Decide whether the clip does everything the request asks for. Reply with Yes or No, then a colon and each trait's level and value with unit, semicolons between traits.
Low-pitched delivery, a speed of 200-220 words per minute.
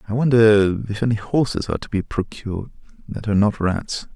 No: low, 105 Hz; average, 190 wpm